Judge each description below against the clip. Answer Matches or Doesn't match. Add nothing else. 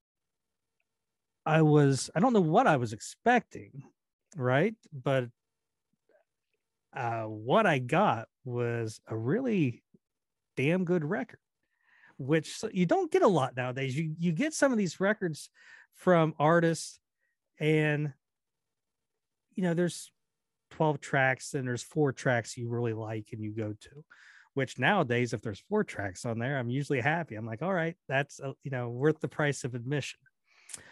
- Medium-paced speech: Matches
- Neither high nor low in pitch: Matches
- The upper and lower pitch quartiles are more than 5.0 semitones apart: Matches